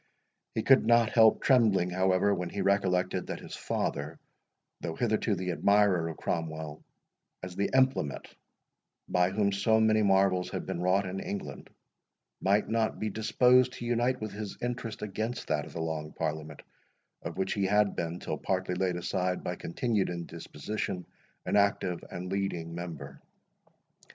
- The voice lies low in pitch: Yes, very low, 95 Hz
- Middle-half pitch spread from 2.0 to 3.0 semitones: No, average, 3.6 semitones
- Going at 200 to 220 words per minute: No, average, 155 wpm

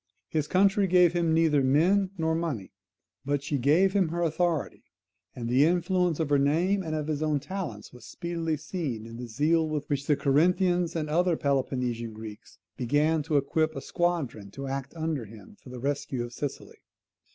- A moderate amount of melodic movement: Yes, average, 4.0 semitones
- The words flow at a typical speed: Yes, average, 185 wpm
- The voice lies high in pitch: No, medium, 155 Hz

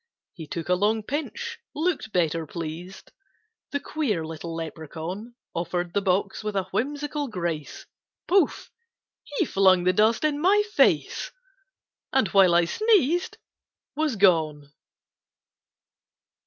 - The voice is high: Yes, high, 195 Hz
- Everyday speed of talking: No, slow, 120 wpm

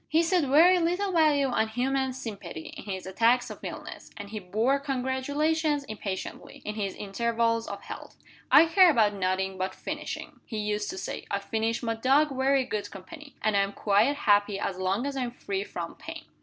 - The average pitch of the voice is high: Yes, high, 235 Hz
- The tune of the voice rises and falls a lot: Yes, wide, 5.8 semitones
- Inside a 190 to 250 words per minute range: Yes, average, 195 wpm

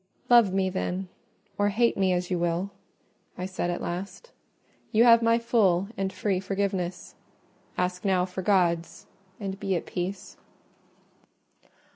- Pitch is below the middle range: No, high, 190 Hz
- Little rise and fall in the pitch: Yes, narrow, 2.0 semitones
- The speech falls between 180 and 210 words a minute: No, average, 140 wpm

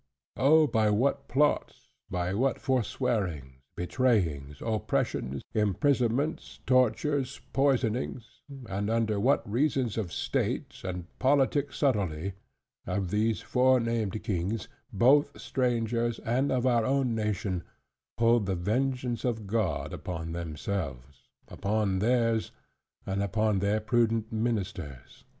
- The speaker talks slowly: Yes, slow, 110 wpm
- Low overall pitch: Yes, low, 110 Hz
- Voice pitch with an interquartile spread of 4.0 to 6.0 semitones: Yes, average, 4.7 semitones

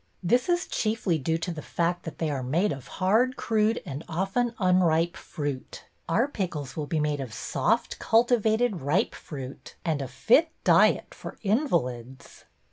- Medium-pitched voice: Yes, medium, 170 Hz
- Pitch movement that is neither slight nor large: No, wide, 7.2 semitones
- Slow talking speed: No, average, 180 wpm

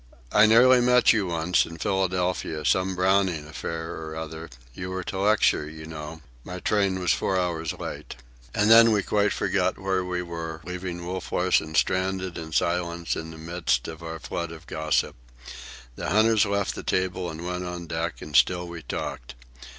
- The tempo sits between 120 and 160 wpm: No, average, 175 wpm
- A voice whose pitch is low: Yes, very low, 90 Hz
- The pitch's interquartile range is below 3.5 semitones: Yes, average, 2.7 semitones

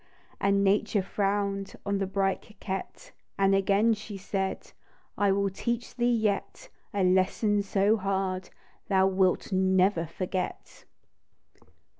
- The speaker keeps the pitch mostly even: Yes, narrow, 1.4 semitones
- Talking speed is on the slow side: Yes, slow, 130 wpm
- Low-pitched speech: No, high, 195 Hz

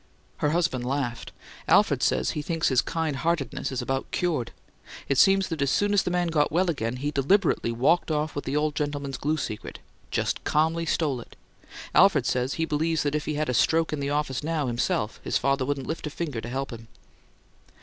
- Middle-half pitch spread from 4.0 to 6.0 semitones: No, average, 3.5 semitones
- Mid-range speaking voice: Yes, medium, 145 Hz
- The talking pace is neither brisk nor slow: No, fast, 210 wpm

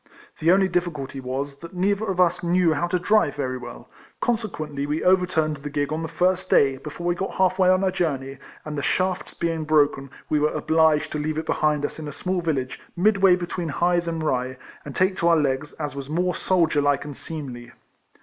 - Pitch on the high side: No, medium, 160 Hz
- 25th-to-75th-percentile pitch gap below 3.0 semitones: No, average, 4.0 semitones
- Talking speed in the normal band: No, fast, 210 wpm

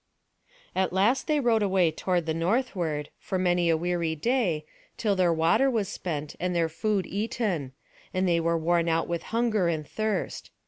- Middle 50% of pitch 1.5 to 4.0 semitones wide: No, average, 4.4 semitones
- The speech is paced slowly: No, average, 175 wpm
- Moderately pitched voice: Yes, medium, 180 Hz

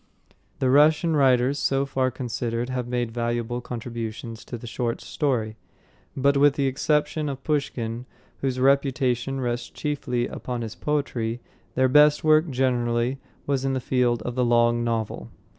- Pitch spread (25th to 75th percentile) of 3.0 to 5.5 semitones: No, narrow, 2.6 semitones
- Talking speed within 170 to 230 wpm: No, average, 150 wpm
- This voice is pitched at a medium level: No, low, 125 Hz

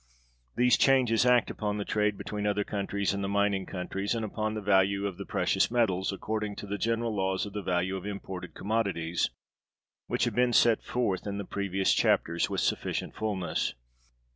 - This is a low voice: Yes, low, 100 Hz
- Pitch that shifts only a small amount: Yes, narrow, 2.1 semitones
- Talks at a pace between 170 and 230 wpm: Yes, average, 185 wpm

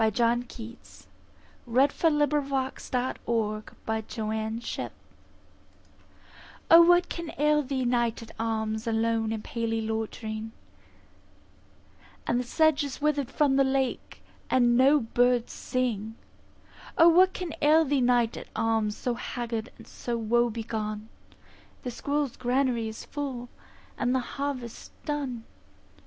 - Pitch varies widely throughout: No, average, 3.7 semitones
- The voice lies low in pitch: No, high, 245 Hz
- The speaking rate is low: Yes, slow, 120 wpm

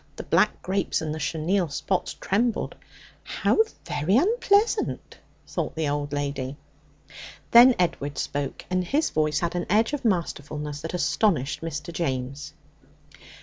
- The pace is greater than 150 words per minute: No, slow, 135 wpm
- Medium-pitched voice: Yes, medium, 165 Hz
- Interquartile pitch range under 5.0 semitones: No, wide, 5.5 semitones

